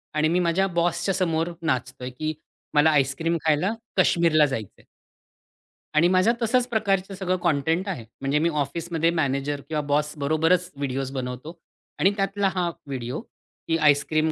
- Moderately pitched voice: Yes, medium, 160 Hz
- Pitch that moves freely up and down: No, average, 4.0 semitones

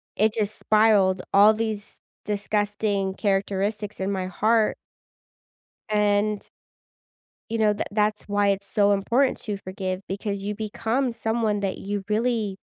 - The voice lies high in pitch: Yes, high, 205 Hz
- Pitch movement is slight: Yes, narrow, 1.5 semitones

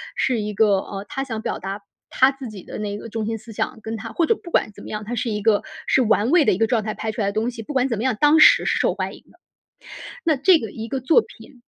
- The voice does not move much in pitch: No, average, 3.8 semitones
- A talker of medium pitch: No, high, 225 Hz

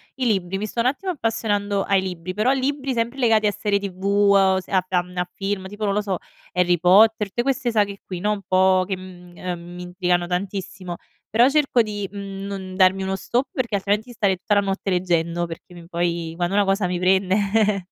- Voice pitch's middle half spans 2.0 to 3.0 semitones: Yes, narrow, 2.6 semitones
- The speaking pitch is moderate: No, high, 195 Hz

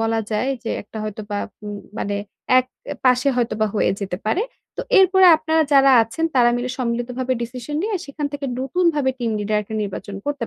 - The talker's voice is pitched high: Yes, very high, 250 Hz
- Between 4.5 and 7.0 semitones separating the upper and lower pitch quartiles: Yes, average, 4.8 semitones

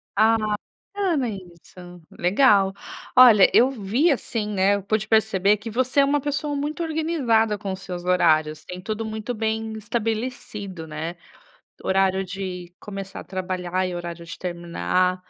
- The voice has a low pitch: No, high, 200 Hz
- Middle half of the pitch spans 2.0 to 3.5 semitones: No, average, 4.0 semitones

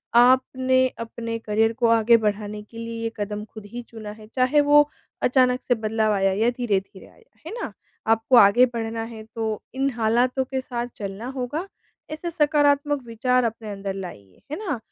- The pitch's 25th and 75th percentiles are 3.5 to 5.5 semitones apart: No, average, 3.1 semitones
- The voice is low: No, high, 230 Hz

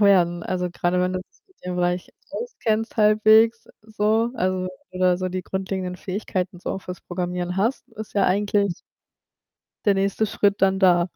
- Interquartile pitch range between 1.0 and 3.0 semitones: Yes, average, 2.7 semitones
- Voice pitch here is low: No, high, 190 Hz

